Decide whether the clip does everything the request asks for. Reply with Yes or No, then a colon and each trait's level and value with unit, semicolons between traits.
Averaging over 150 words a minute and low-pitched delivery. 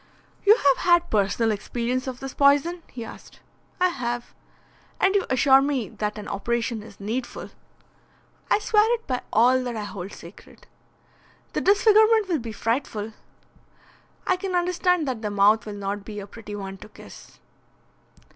No: average, 160 wpm; high, 245 Hz